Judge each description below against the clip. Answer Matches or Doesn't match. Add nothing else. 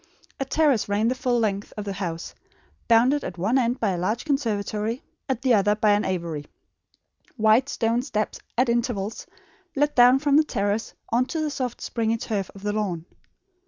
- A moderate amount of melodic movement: Matches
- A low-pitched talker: Doesn't match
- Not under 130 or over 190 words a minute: Matches